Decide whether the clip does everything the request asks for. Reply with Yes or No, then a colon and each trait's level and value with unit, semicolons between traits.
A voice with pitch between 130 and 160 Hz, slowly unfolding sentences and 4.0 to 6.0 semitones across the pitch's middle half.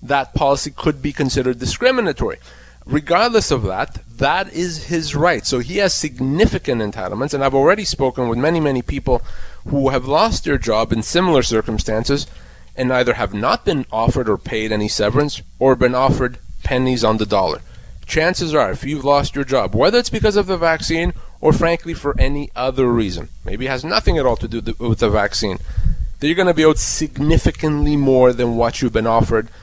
No: low, 135 Hz; average, 190 wpm; wide, 5.4 semitones